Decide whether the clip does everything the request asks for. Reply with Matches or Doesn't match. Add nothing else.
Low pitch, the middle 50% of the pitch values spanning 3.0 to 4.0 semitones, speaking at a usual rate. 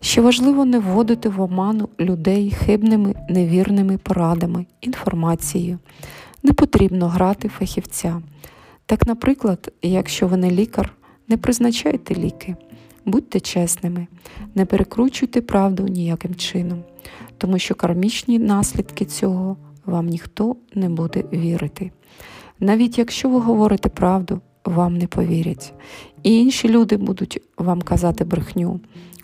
Doesn't match